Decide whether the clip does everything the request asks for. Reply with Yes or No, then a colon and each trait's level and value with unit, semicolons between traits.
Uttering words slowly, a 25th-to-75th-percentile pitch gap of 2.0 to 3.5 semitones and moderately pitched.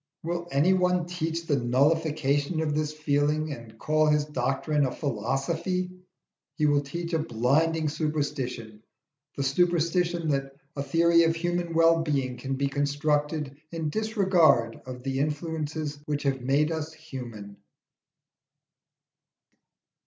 Yes: slow, 125 wpm; average, 3.2 semitones; medium, 150 Hz